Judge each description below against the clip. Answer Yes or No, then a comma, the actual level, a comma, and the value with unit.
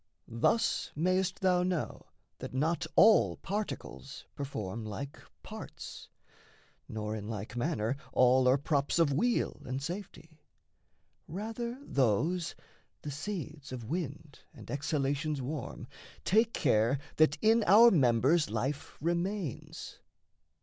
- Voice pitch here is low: No, medium, 150 Hz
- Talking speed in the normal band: No, slow, 115 wpm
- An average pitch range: No, wide, 5.9 semitones